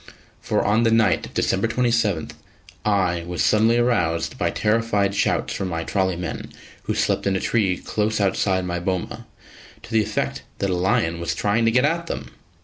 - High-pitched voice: No, low, 100 Hz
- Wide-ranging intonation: No, average, 3.9 semitones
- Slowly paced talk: No, average, 185 wpm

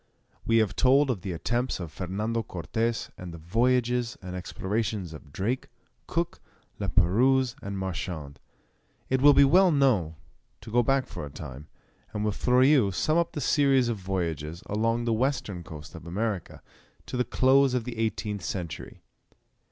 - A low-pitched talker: Yes, low, 110 Hz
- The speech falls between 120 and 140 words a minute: No, average, 165 wpm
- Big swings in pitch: Yes, wide, 5.9 semitones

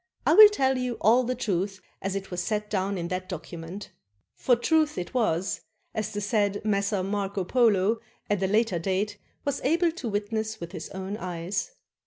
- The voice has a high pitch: Yes, high, 205 Hz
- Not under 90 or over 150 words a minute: No, average, 190 wpm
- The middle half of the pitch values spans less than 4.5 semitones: Yes, average, 3.7 semitones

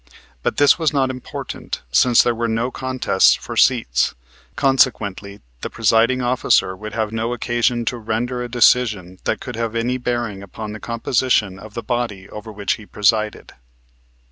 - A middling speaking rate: Yes, average, 165 wpm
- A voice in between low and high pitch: No, low, 115 Hz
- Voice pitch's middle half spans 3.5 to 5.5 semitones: No, narrow, 2.6 semitones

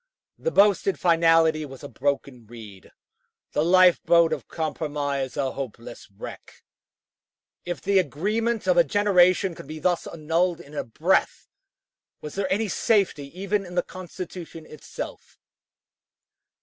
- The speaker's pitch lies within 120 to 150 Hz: No, medium, 165 Hz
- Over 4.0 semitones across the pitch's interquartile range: Yes, average, 4.4 semitones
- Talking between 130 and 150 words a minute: Yes, slow, 135 wpm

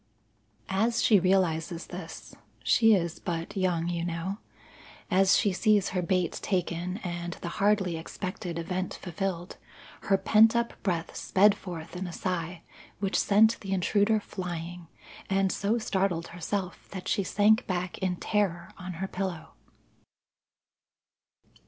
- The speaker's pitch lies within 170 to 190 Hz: Yes, medium, 185 Hz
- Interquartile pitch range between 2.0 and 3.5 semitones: Yes, narrow, 2.5 semitones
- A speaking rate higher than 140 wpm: No, slow, 135 wpm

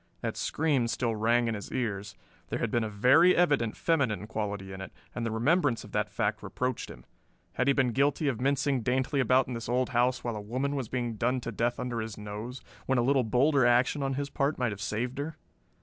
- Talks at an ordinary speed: No, fast, 225 wpm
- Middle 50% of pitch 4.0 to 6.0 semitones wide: No, average, 3.3 semitones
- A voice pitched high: No, low, 125 Hz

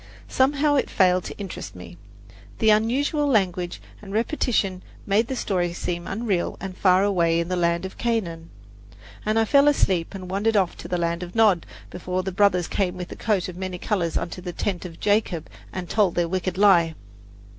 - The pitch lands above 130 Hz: Yes, medium, 185 Hz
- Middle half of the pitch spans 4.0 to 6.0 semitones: No, average, 3.3 semitones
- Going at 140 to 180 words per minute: No, average, 190 wpm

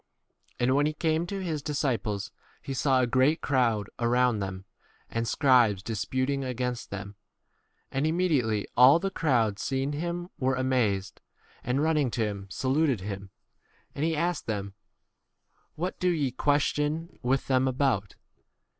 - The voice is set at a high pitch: No, low, 130 Hz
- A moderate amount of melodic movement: Yes, average, 5.0 semitones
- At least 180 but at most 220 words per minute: No, average, 165 wpm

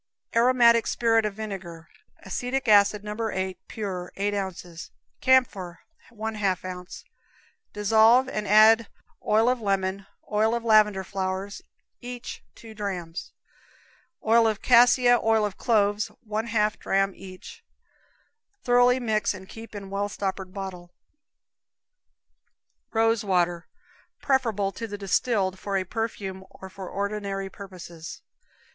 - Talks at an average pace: No, slow, 110 wpm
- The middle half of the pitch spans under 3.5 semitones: Yes, average, 2.9 semitones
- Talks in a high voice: Yes, high, 205 Hz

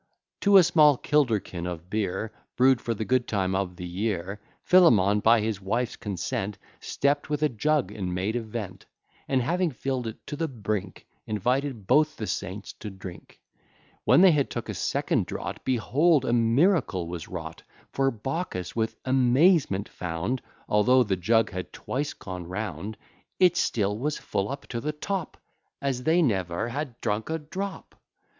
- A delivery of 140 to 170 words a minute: Yes, average, 165 wpm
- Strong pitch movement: Yes, wide, 6.4 semitones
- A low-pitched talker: Yes, low, 115 Hz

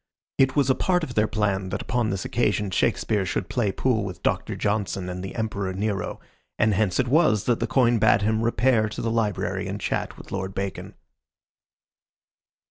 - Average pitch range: Yes, average, 3.3 semitones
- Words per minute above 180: Yes, average, 190 wpm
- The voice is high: No, low, 110 Hz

